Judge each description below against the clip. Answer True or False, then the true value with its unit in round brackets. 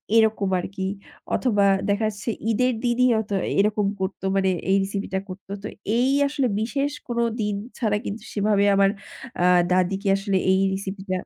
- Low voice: False (205 Hz)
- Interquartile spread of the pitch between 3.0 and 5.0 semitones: False (2.4 semitones)